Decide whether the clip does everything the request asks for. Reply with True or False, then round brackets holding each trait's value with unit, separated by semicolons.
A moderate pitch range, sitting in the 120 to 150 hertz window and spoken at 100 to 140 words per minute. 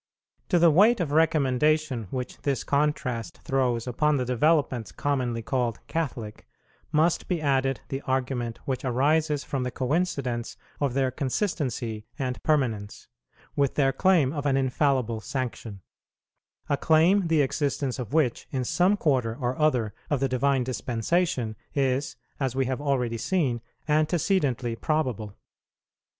True (3.6 semitones; 135 Hz; 135 wpm)